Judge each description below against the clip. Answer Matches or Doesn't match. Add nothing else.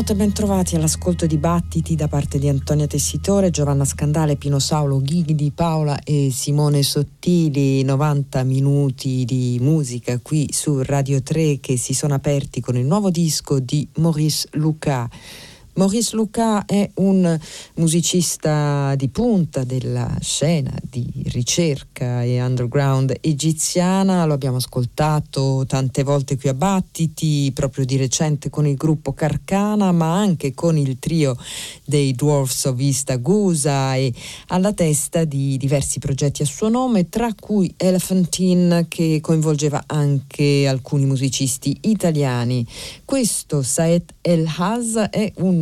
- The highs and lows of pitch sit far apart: Doesn't match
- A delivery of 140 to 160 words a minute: Doesn't match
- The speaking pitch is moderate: Matches